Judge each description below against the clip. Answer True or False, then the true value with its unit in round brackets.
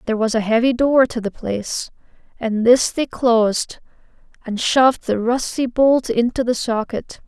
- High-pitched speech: True (240 Hz)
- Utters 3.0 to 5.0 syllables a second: True (4.7 syllables/s)